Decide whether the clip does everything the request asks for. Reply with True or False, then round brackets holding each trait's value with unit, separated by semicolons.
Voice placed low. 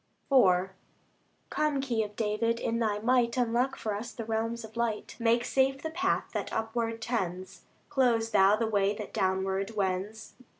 False (225 Hz)